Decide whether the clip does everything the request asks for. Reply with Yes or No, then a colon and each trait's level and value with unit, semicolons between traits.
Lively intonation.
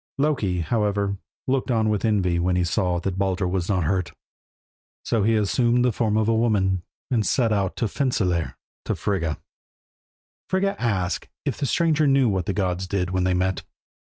No: average, 4.1 semitones